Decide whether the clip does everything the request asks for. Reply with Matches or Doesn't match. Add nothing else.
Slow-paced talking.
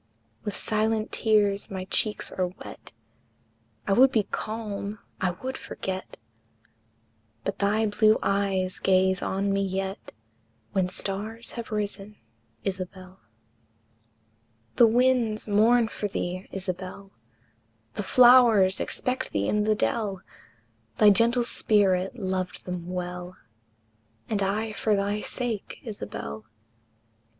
Matches